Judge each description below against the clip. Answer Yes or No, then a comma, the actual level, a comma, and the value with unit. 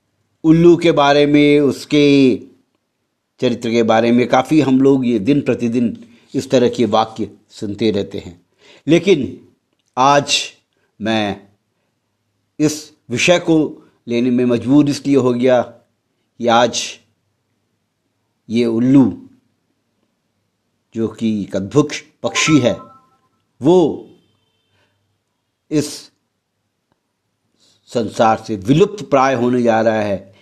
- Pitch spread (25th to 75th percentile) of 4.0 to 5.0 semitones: Yes, average, 4.6 semitones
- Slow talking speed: Yes, slow, 105 wpm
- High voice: No, low, 120 Hz